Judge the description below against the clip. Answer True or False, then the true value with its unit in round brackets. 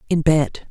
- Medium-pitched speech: True (155 Hz)